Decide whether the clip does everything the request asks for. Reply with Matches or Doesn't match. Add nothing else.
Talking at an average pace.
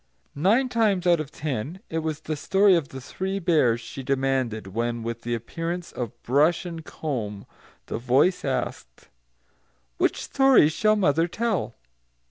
Matches